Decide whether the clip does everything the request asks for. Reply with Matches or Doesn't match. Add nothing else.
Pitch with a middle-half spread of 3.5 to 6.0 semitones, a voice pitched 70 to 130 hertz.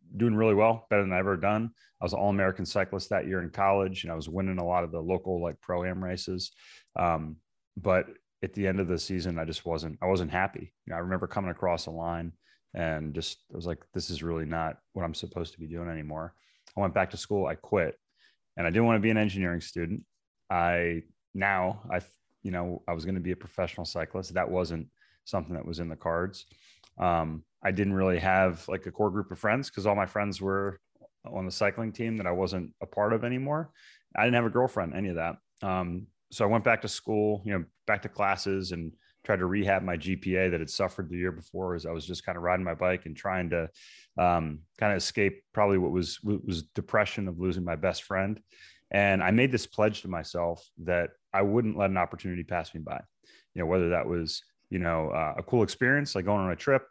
Doesn't match